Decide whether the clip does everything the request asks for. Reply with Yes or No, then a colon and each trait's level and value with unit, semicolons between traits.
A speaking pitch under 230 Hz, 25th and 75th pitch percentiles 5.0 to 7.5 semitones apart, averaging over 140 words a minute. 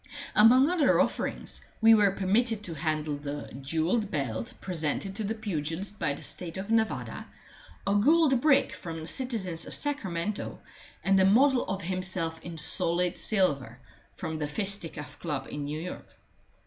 Yes: medium, 185 Hz; wide, 5.5 semitones; average, 155 wpm